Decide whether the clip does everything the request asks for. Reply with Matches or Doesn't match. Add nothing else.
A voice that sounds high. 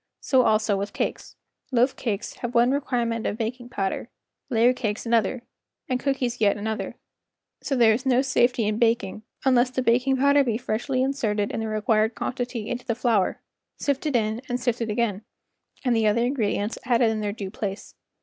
Matches